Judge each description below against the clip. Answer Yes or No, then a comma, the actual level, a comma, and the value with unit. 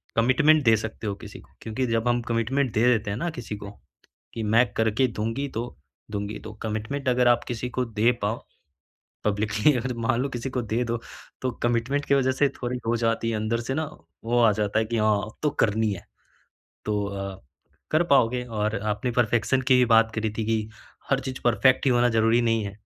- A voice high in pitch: No, low, 115 Hz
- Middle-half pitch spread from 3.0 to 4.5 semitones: No, narrow, 2.6 semitones